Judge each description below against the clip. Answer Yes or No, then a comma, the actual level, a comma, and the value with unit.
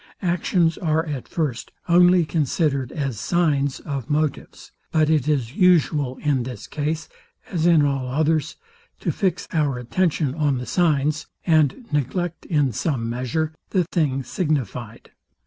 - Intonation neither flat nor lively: Yes, average, 3.5 semitones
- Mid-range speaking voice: Yes, medium, 150 Hz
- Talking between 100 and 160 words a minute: Yes, average, 140 wpm